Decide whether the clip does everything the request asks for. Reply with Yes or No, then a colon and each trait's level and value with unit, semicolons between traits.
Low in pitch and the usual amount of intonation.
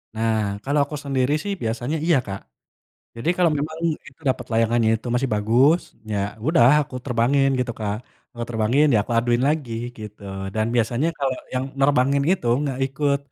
Yes: low, 130 Hz; average, 3.7 semitones